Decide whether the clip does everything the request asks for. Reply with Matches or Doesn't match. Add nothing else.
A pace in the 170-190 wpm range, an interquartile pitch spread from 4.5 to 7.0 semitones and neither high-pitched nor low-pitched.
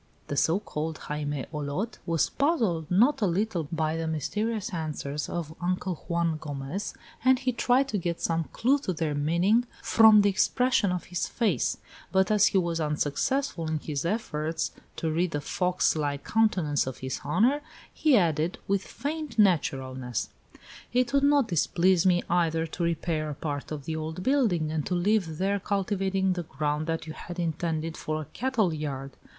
Matches